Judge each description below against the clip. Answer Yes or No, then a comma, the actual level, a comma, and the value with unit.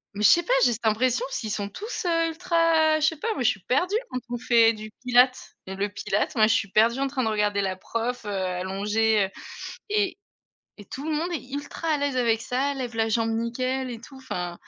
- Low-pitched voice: No, high, 240 Hz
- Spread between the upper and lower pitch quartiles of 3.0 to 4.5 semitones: No, average, 5.1 semitones